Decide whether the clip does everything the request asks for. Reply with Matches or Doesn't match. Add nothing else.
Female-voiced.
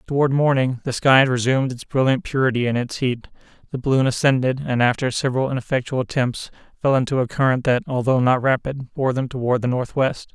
Doesn't match